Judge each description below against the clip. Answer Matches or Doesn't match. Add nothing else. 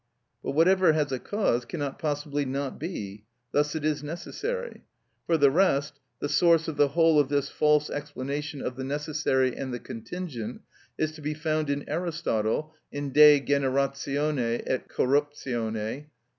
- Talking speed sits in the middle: Matches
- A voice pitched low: Doesn't match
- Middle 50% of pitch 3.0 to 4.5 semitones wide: Doesn't match